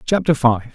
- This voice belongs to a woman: No, male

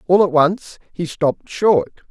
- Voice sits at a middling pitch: Yes, medium, 165 Hz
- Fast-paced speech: No, average, 170 wpm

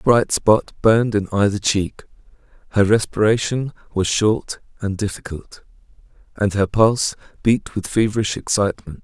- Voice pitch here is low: Yes, low, 105 Hz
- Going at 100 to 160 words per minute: Yes, slow, 135 wpm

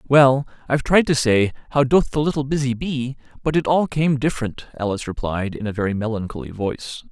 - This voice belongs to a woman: No, male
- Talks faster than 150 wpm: Yes, average, 195 wpm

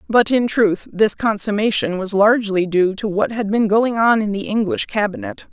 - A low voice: No, high, 210 Hz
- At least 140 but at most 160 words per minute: No, average, 195 wpm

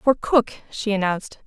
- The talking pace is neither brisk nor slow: Yes, average, 165 wpm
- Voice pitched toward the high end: Yes, high, 215 Hz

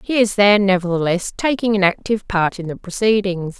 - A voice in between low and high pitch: No, high, 200 Hz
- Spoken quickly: No, average, 185 wpm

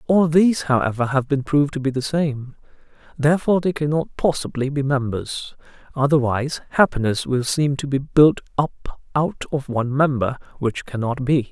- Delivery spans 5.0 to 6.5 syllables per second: Yes, 5.2 syllables/s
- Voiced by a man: Yes, male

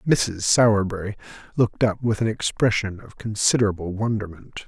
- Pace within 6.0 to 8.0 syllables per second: No, 5.4 syllables/s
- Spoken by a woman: No, male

